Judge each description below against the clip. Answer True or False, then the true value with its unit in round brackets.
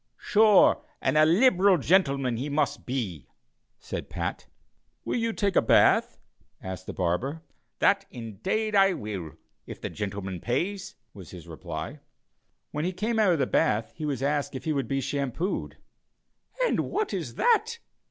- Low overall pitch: False (145 Hz)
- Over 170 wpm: False (160 wpm)